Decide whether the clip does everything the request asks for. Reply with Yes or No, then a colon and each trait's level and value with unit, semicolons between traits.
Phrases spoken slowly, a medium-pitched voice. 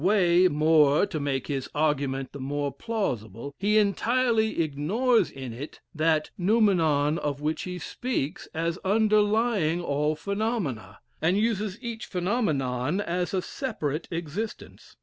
Yes: slow, 130 wpm; medium, 170 Hz